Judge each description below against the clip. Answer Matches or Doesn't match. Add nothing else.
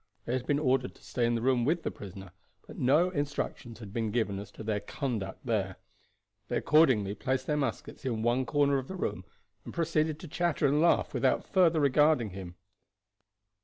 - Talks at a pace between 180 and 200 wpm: Matches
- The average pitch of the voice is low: Matches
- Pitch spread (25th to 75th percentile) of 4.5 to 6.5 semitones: Matches